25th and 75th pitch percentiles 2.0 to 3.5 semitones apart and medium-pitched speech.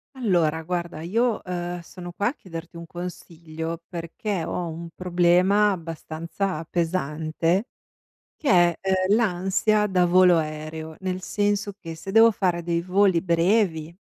Yes: narrow, 2.6 semitones; medium, 175 Hz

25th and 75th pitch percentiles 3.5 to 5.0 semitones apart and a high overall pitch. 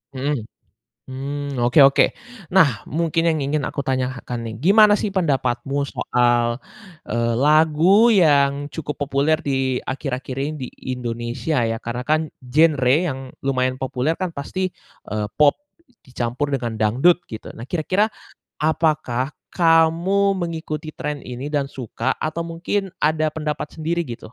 No: average, 4.1 semitones; medium, 145 Hz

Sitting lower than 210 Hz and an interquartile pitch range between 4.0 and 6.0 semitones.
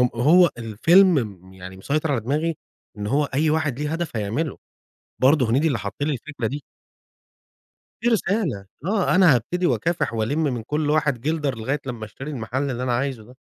Yes: medium, 140 Hz; average, 5.1 semitones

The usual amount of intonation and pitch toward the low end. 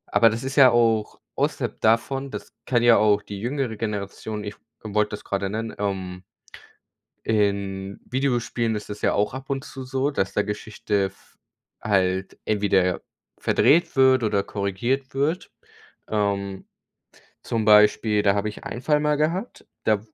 Yes: average, 4.5 semitones; low, 110 Hz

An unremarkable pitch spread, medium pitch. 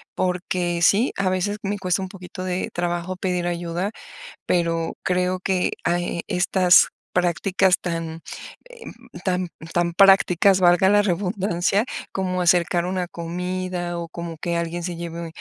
No: narrow, 1.3 semitones; medium, 180 Hz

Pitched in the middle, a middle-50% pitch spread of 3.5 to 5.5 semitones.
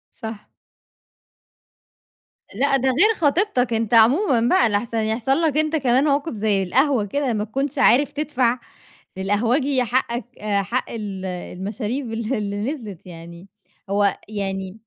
No: high, 230 Hz; average, 4.9 semitones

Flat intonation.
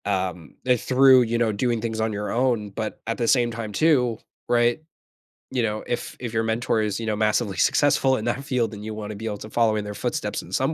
Yes: narrow, 2.2 semitones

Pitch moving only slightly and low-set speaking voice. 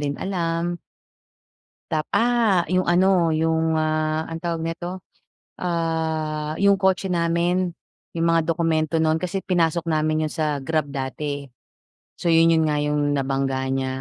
No: narrow, 1.9 semitones; medium, 165 Hz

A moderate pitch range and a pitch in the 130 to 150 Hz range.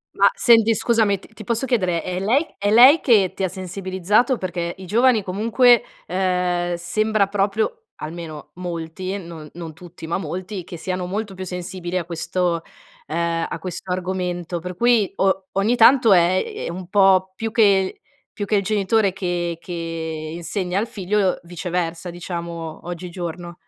No: average, 3.0 semitones; medium, 185 Hz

